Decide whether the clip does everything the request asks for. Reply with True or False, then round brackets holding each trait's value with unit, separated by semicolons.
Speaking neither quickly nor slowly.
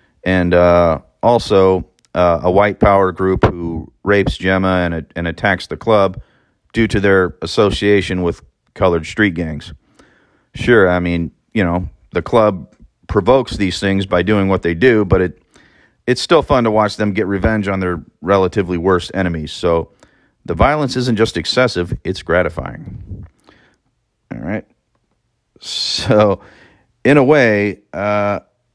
True (145 wpm)